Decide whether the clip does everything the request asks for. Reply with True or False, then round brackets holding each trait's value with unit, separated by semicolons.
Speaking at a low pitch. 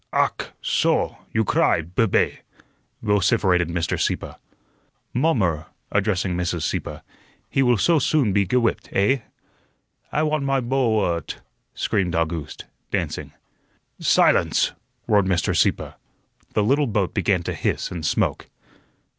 True (100 Hz)